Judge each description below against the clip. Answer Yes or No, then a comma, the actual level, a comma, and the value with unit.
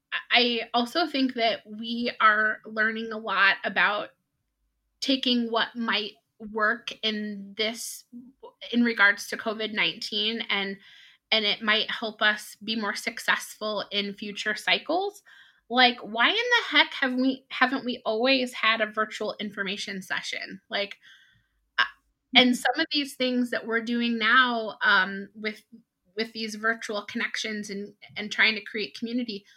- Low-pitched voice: No, high, 225 Hz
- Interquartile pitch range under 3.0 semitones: Yes, narrow, 2.5 semitones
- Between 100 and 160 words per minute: Yes, average, 140 wpm